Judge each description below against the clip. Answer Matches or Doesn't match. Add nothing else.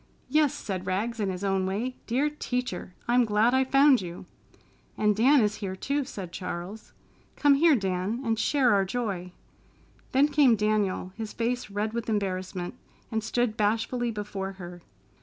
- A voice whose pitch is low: Doesn't match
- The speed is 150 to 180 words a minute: Matches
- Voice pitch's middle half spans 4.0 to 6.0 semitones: Matches